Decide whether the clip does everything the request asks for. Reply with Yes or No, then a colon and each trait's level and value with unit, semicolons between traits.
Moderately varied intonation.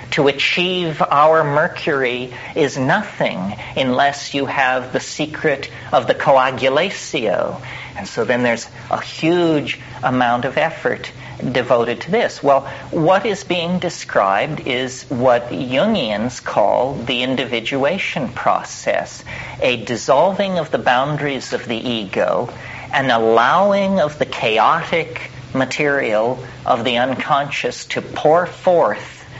Yes: average, 4.4 semitones